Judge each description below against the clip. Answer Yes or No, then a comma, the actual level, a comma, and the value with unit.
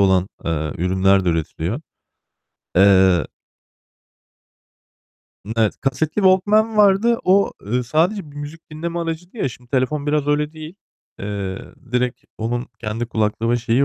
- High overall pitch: No, low, 125 Hz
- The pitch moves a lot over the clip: Yes, wide, 8.2 semitones